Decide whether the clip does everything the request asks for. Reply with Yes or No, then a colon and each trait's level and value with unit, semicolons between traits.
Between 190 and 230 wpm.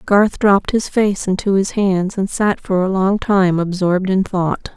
Yes: average, 200 wpm